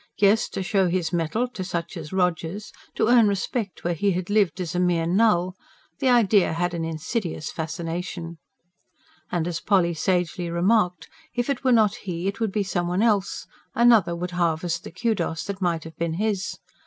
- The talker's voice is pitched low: No, medium, 180 Hz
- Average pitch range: Yes, average, 3.4 semitones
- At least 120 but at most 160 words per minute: No, average, 185 wpm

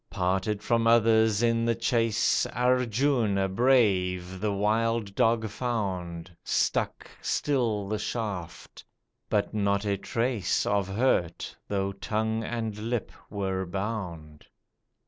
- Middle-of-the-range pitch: No, low, 105 Hz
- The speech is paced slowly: Yes, slow, 110 wpm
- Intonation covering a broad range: No, average, 3.0 semitones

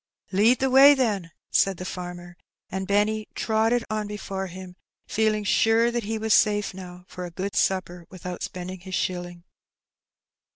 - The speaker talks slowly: No, average, 160 wpm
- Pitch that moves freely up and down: No, average, 3.2 semitones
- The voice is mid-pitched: No, high, 195 Hz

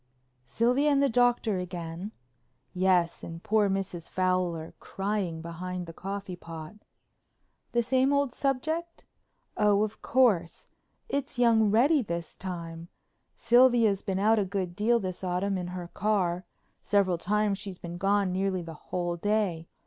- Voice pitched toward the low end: No, high, 195 Hz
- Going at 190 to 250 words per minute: No, average, 140 wpm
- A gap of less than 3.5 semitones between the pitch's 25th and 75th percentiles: No, average, 3.9 semitones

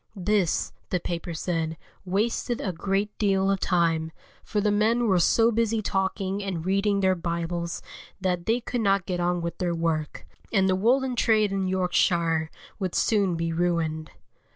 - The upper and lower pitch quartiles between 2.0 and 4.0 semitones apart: Yes, average, 3.3 semitones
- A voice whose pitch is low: No, high, 190 Hz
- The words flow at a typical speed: Yes, average, 165 wpm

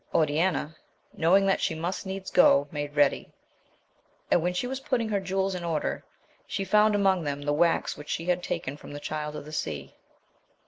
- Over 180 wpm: Yes, average, 195 wpm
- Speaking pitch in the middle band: Yes, medium, 170 Hz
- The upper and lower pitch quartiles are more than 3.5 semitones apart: Yes, average, 4.5 semitones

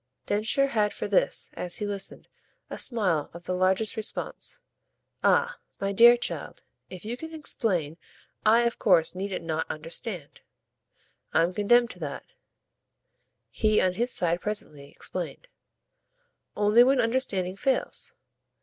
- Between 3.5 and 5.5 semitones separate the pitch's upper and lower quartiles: Yes, average, 4.7 semitones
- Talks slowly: Yes, slow, 130 wpm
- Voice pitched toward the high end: Yes, high, 210 Hz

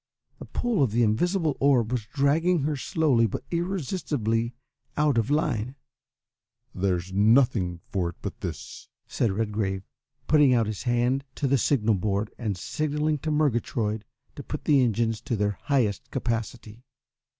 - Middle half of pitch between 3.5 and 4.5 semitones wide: No, average, 5.3 semitones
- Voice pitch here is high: No, low, 120 Hz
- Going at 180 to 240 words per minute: No, average, 150 wpm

